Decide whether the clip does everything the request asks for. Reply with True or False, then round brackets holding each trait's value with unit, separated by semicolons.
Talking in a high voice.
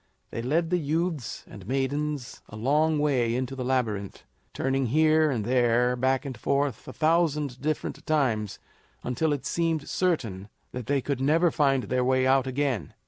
False (135 Hz)